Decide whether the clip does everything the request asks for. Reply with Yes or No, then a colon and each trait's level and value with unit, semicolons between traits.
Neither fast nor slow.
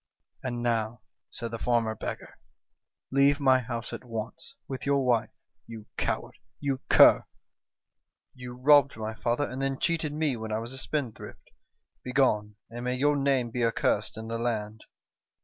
Yes: average, 160 wpm